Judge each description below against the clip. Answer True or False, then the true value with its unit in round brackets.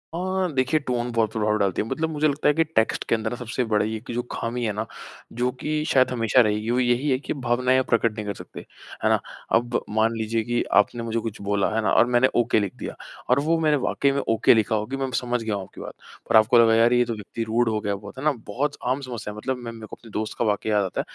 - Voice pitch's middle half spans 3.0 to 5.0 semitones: False (2.6 semitones)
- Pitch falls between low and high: False (115 Hz)